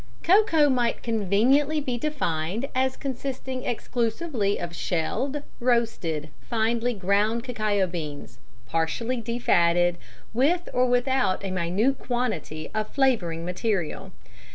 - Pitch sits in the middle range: No, high, 230 Hz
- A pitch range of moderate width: No, wide, 6.3 semitones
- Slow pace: Yes, slow, 110 wpm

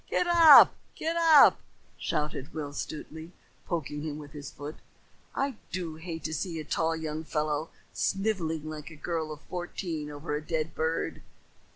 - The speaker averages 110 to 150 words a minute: No, average, 160 wpm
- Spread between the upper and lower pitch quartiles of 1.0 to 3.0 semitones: Yes, narrow, 2.5 semitones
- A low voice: No, medium, 160 Hz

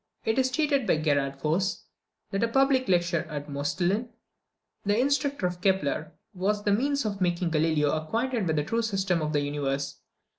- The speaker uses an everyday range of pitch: No, wide, 6.9 semitones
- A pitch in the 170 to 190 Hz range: Yes, medium, 185 Hz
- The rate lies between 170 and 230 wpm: Yes, average, 175 wpm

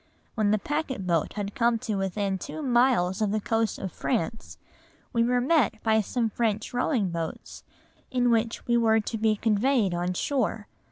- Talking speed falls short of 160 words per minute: No, average, 175 wpm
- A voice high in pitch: Yes, high, 220 Hz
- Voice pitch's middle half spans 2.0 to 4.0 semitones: Yes, average, 3.2 semitones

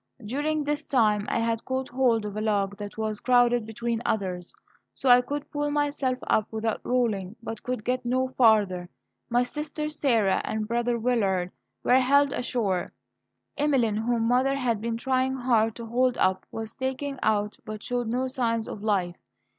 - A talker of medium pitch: No, high, 235 Hz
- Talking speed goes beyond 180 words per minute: No, average, 170 wpm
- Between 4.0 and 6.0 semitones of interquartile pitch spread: No, average, 3.2 semitones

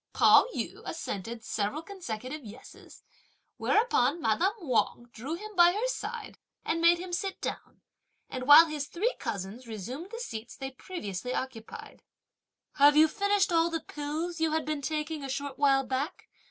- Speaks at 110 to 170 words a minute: Yes, average, 160 wpm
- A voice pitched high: Yes, very high, 295 Hz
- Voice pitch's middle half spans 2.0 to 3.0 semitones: No, wide, 5.4 semitones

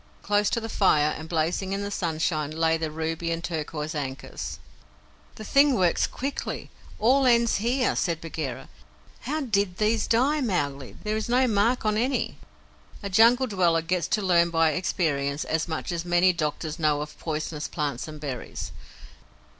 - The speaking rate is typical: Yes, average, 165 wpm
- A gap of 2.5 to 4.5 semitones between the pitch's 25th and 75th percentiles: No, wide, 5.6 semitones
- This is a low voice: No, medium, 175 Hz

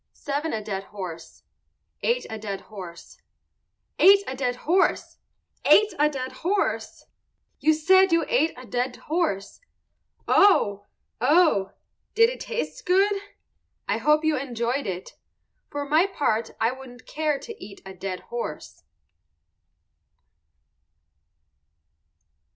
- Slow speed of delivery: Yes, slow, 120 wpm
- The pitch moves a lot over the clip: Yes, wide, 8.6 semitones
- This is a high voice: Yes, very high, 275 Hz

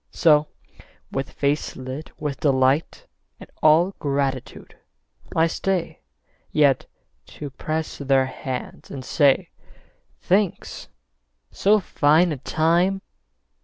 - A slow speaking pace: Yes, slow, 100 wpm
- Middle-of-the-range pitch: Yes, medium, 150 Hz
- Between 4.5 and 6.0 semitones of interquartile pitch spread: No, average, 3.5 semitones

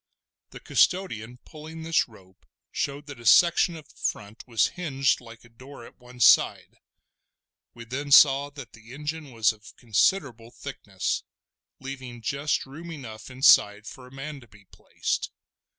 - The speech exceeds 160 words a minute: No, average, 155 wpm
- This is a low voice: Yes, low, 130 Hz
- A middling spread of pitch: Yes, average, 4.1 semitones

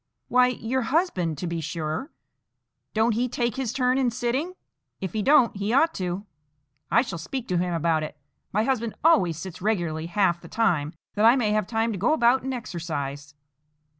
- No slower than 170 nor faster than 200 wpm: Yes, average, 190 wpm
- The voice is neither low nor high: No, high, 215 Hz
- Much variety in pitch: Yes, wide, 6.6 semitones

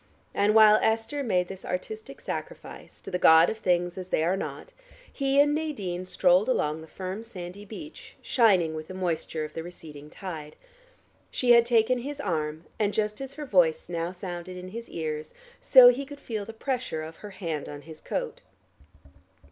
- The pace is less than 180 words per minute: No, average, 185 wpm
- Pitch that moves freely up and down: Yes, wide, 5.8 semitones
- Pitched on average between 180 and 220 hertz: Yes, high, 190 Hz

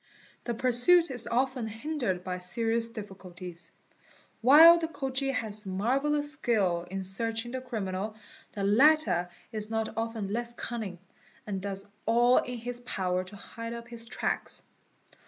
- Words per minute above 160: No, average, 140 wpm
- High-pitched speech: Yes, high, 230 Hz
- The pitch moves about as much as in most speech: Yes, average, 4.0 semitones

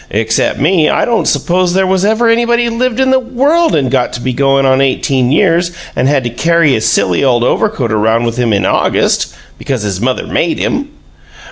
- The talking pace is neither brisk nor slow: No, fast, 210 wpm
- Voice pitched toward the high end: No, medium, 145 Hz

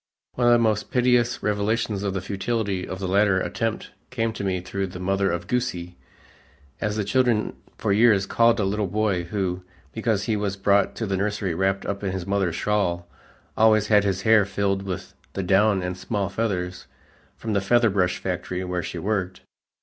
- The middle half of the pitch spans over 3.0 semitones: No, narrow, 2.5 semitones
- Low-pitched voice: Yes, low, 100 Hz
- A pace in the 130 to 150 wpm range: No, average, 190 wpm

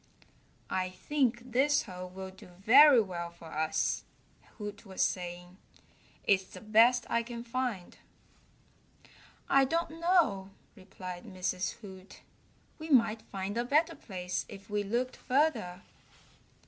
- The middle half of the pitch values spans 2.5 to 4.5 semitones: No, average, 5.3 semitones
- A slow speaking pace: Yes, slow, 125 wpm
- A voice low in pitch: No, high, 205 Hz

